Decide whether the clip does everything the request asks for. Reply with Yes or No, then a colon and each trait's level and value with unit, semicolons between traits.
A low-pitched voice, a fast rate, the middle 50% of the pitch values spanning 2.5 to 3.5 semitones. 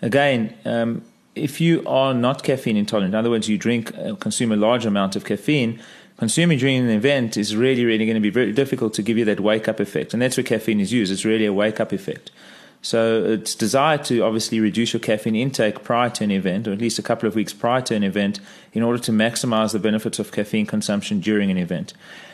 Yes: low, 115 Hz; fast, 235 wpm; average, 2.8 semitones